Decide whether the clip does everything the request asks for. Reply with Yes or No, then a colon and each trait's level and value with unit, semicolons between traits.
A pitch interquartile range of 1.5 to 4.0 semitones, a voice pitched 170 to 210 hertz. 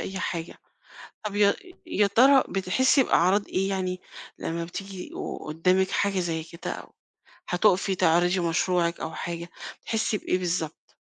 Yes: average, 2.7 semitones; medium, 185 Hz